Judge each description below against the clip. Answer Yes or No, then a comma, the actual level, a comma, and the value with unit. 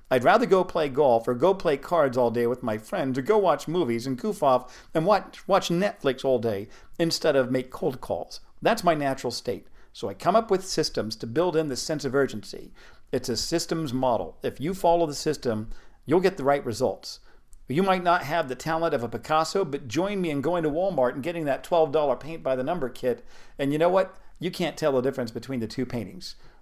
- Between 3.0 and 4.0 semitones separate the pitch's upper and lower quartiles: No, wide, 5.4 semitones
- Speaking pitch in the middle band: Yes, medium, 150 Hz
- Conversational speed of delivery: No, fast, 230 wpm